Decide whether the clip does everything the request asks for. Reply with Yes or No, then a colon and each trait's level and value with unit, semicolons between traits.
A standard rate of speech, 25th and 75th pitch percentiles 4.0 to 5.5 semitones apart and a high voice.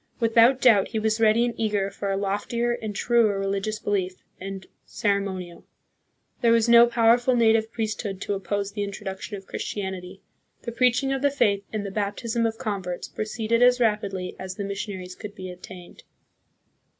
No: average, 170 wpm; average, 2.9 semitones; high, 210 Hz